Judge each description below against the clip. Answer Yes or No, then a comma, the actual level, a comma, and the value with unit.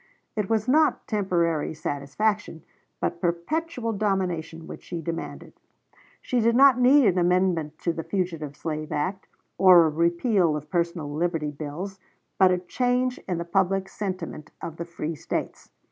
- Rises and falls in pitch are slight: No, average, 4.0 semitones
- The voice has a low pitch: No, medium, 180 Hz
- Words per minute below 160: Yes, average, 150 wpm